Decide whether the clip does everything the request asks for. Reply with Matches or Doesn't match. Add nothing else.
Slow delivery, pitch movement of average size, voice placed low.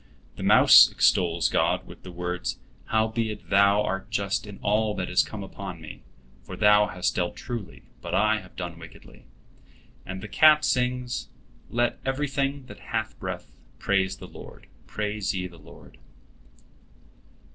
Doesn't match